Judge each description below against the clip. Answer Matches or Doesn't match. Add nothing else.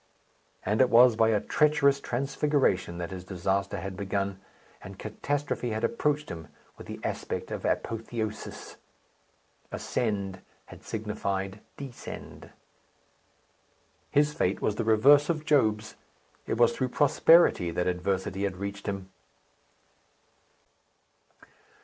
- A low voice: Matches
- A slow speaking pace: Matches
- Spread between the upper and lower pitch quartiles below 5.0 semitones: Doesn't match